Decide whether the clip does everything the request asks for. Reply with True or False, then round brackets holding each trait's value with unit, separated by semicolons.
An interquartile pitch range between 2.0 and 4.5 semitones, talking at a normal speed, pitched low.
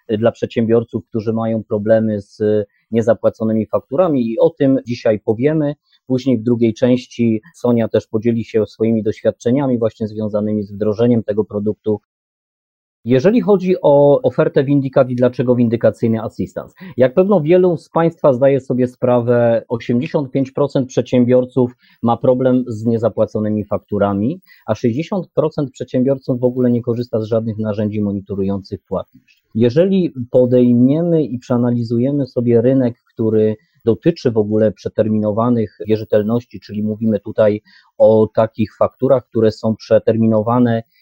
True (3.2 semitones; 125 wpm; 120 Hz)